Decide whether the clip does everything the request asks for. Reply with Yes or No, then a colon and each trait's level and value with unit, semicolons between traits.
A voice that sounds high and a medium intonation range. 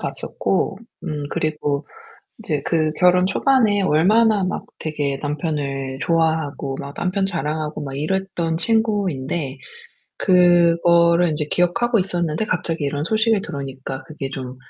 No: medium, 165 Hz; average, 4.4 semitones